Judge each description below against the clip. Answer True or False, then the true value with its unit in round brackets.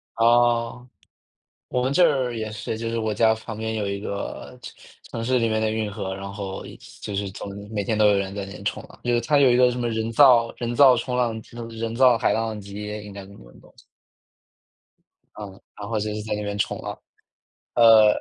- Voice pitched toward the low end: True (110 Hz)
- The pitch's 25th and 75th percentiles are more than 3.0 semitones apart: False (2.5 semitones)